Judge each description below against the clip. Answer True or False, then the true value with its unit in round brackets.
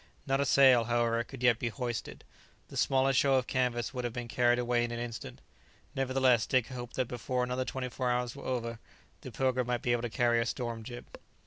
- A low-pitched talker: True (125 Hz)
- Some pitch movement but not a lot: False (1.5 semitones)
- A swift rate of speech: True (220 wpm)